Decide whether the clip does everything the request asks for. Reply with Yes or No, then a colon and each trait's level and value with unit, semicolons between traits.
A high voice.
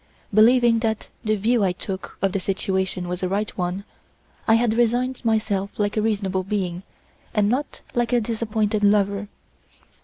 Yes: high, 210 Hz